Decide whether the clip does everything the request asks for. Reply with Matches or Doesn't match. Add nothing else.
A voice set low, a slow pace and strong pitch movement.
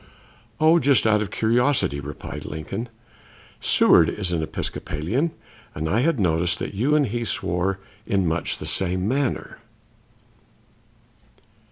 Matches